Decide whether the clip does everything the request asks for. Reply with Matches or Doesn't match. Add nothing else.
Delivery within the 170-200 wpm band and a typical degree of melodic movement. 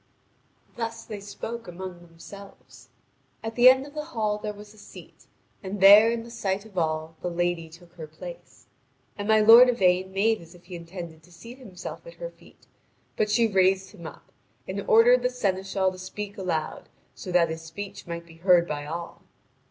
Matches